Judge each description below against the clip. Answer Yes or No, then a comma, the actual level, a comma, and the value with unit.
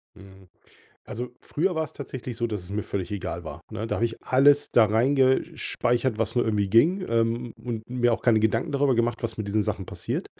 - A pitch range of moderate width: Yes, average, 3.2 semitones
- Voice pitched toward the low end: Yes, low, 115 Hz